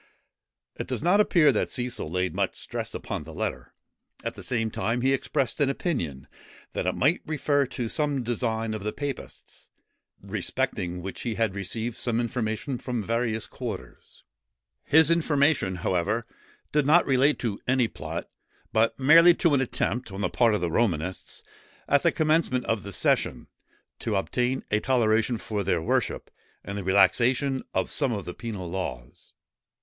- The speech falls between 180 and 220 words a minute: No, average, 165 wpm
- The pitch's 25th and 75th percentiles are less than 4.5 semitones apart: No, average, 5.2 semitones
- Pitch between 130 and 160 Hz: No, low, 120 Hz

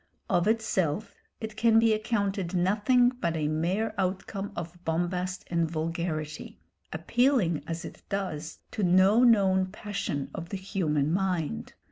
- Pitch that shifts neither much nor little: Yes, average, 4.2 semitones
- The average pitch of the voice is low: No, medium, 185 Hz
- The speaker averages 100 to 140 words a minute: Yes, slow, 135 wpm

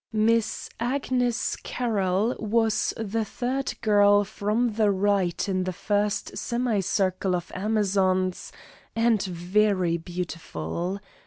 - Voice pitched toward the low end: No, high, 205 Hz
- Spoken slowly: Yes, slow, 105 wpm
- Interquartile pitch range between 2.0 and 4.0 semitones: Yes, average, 3.3 semitones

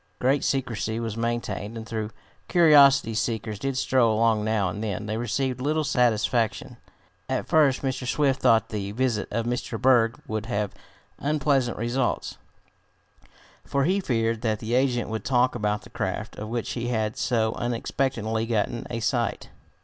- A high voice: No, low, 115 Hz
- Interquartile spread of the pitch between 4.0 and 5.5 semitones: No, average, 2.9 semitones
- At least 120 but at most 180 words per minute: Yes, average, 160 wpm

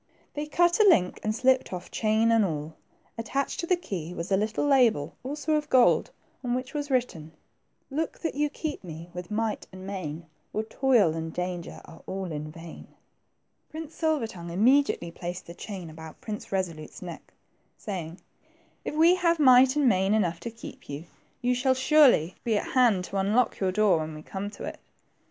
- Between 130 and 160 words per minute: No, average, 190 wpm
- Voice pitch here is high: Yes, high, 215 Hz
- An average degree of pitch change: No, wide, 7.3 semitones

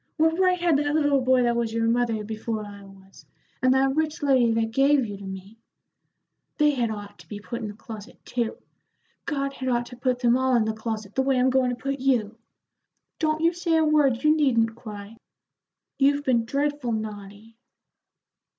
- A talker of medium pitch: No, high, 245 Hz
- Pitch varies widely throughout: No, average, 4.1 semitones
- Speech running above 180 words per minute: Yes, average, 195 wpm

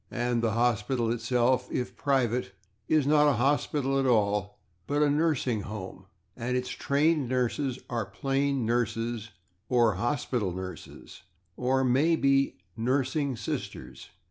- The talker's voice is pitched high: No, low, 125 Hz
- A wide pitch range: No, average, 3.2 semitones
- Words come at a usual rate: No, slow, 125 wpm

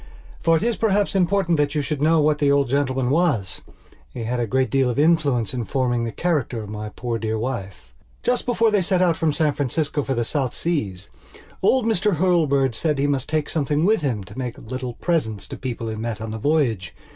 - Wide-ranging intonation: Yes, wide, 5.7 semitones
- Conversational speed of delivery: No, fast, 220 wpm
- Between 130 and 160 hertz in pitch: Yes, medium, 140 Hz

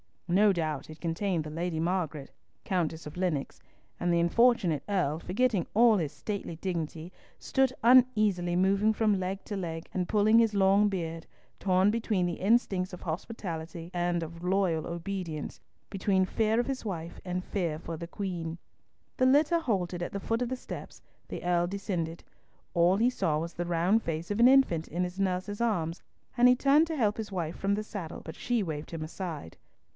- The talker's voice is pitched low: No, medium, 185 Hz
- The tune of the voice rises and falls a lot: No, average, 4.0 semitones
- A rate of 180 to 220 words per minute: Yes, average, 185 wpm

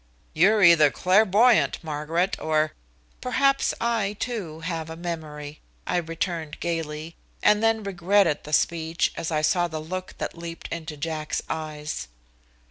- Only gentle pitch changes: No, average, 3.5 semitones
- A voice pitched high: No, medium, 165 Hz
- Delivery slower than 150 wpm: Yes, average, 140 wpm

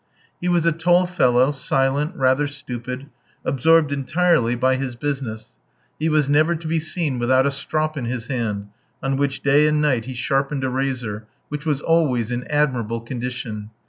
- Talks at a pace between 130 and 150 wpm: No, average, 175 wpm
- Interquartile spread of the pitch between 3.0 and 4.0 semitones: Yes, average, 3.4 semitones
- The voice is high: No, low, 135 Hz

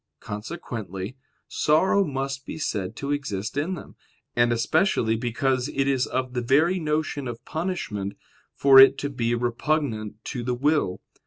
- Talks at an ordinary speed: Yes, average, 150 wpm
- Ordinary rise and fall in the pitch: Yes, average, 4.3 semitones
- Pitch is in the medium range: No, low, 130 Hz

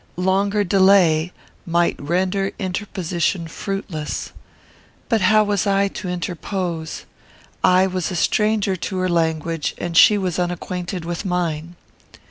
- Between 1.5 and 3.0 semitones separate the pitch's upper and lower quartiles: Yes, narrow, 2.5 semitones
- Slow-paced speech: Yes, slow, 120 wpm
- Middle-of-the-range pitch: Yes, medium, 180 Hz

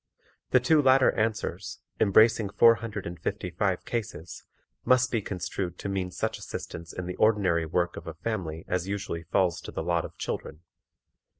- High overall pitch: No, very low, 95 Hz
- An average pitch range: Yes, average, 4.6 semitones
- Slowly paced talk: No, average, 175 wpm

